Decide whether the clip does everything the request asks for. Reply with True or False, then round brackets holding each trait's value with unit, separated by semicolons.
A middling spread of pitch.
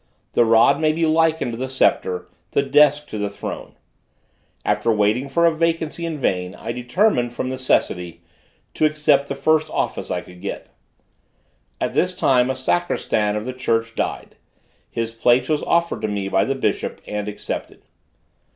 False (6.1 semitones)